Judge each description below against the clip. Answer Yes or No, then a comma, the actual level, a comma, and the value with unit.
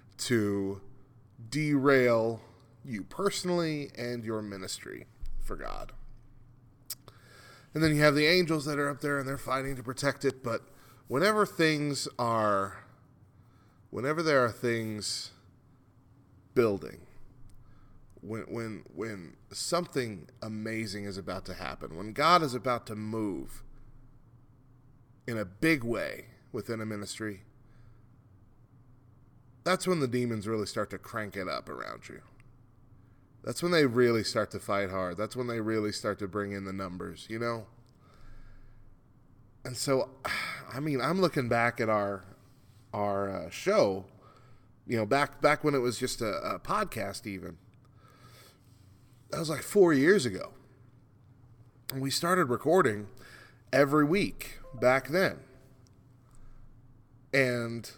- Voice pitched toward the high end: No, low, 120 Hz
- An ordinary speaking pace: No, slow, 130 wpm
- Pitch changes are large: No, average, 3.3 semitones